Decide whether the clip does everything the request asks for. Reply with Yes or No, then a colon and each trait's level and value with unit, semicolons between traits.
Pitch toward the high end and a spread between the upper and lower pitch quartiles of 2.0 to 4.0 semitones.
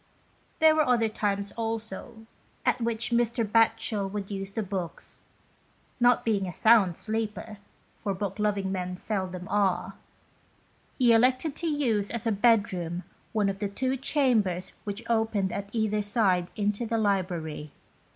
Yes: high, 210 Hz; average, 2.9 semitones